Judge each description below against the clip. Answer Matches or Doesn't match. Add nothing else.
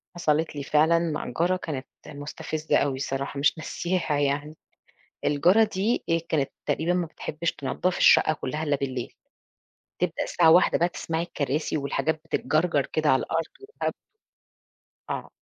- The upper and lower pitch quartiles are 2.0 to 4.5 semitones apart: Matches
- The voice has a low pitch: Doesn't match